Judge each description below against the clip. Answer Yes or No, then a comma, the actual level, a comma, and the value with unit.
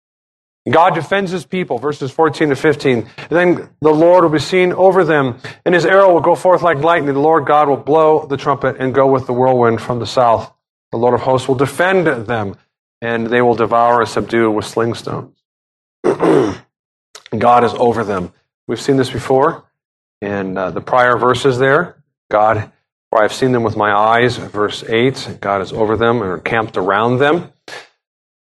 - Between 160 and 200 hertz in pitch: No, low, 130 Hz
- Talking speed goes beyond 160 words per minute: Yes, average, 185 wpm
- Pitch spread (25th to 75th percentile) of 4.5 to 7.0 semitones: Yes, average, 5.0 semitones